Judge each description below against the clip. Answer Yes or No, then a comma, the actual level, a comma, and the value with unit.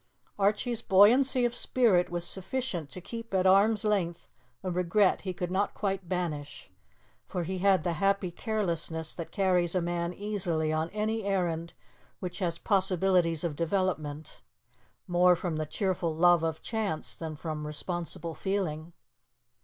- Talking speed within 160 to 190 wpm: No, average, 145 wpm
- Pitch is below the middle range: No, medium, 180 Hz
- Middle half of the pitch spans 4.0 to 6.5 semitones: No, average, 3.0 semitones